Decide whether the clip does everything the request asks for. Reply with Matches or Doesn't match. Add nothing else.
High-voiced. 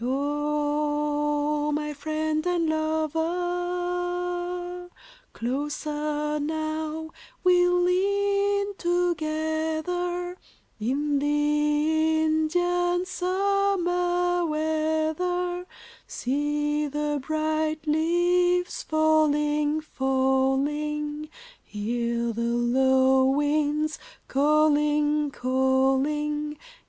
Matches